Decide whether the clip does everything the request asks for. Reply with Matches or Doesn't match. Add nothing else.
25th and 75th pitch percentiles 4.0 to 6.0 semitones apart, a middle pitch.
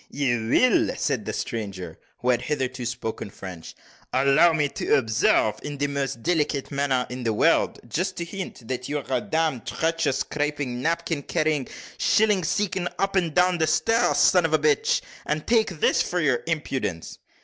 Matches